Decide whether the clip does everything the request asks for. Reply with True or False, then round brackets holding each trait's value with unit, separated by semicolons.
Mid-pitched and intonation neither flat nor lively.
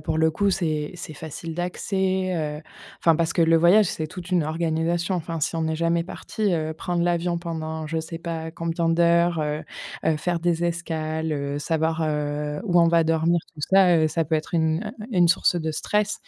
False (165 Hz; 1.5 semitones)